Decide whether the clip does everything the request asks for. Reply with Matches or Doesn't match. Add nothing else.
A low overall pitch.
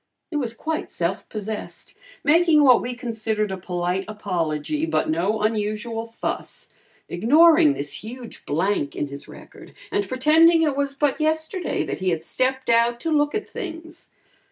Doesn't match